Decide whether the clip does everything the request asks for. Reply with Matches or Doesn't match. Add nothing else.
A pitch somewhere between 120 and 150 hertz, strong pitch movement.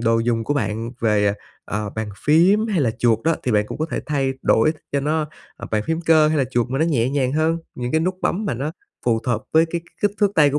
Matches